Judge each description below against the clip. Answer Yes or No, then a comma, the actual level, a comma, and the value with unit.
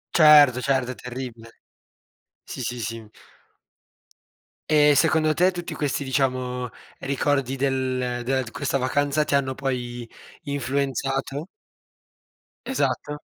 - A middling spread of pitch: No, narrow, 2.3 semitones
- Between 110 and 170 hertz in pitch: Yes, low, 135 Hz